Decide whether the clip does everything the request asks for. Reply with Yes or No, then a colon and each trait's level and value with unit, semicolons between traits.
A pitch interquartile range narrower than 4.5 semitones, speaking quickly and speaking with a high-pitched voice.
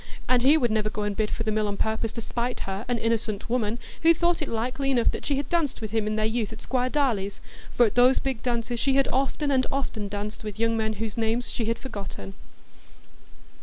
Yes: average, 3.1 semitones; fast, 240 wpm; high, 230 Hz